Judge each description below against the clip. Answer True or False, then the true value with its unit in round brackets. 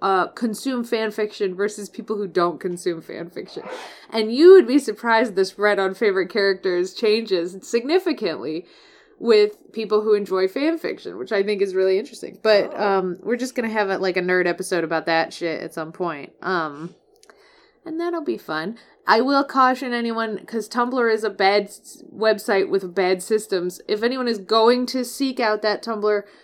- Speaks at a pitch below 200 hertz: False (210 Hz)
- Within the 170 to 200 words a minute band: True (175 wpm)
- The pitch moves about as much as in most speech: True (4.1 semitones)